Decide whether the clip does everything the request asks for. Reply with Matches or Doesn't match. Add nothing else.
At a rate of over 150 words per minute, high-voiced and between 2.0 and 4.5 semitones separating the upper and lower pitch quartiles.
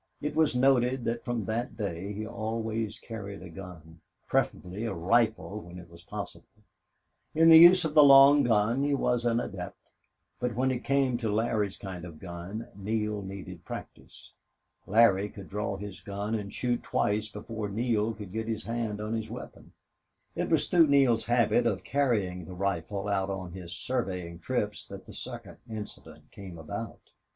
Doesn't match